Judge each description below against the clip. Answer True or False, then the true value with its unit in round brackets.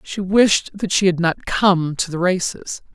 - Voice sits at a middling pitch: True (180 Hz)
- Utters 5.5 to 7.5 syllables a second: False (4.0 syllables/s)